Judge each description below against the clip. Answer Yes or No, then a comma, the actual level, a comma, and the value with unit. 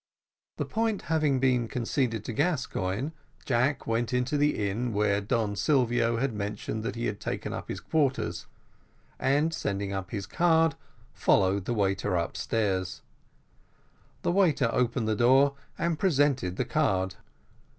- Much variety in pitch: Yes, wide, 5.8 semitones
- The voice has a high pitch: No, low, 120 Hz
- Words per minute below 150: Yes, average, 140 wpm